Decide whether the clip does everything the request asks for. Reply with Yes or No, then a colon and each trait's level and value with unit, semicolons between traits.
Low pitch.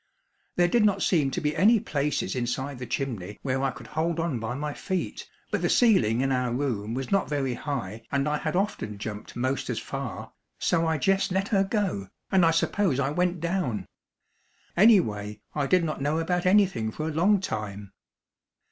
No: medium, 150 Hz